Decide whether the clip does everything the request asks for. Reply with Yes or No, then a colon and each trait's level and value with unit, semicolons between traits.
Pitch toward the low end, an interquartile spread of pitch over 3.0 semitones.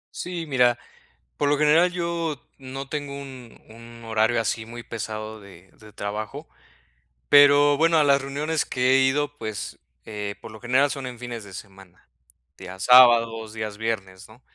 Yes: low, 120 Hz; average, 4.7 semitones